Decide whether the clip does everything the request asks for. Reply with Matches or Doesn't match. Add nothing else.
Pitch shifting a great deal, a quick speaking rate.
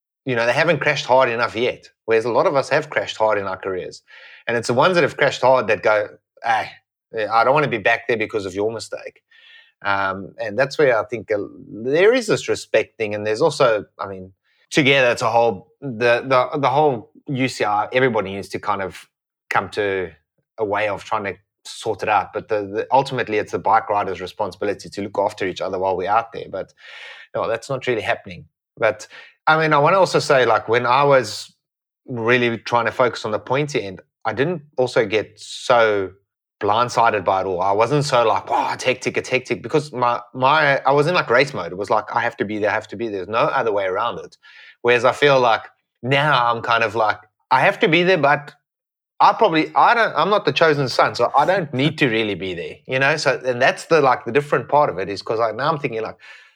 Matches